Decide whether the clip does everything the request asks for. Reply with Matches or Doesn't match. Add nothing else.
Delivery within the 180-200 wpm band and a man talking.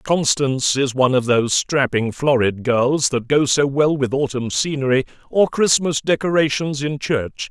Doesn't match